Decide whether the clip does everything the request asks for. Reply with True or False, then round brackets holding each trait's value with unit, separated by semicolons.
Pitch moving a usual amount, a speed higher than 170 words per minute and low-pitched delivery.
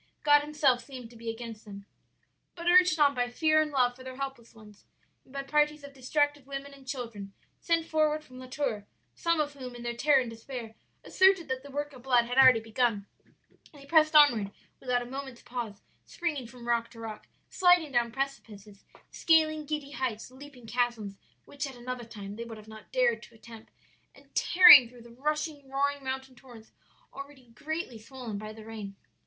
False (3.9 semitones; 190 wpm; 260 Hz)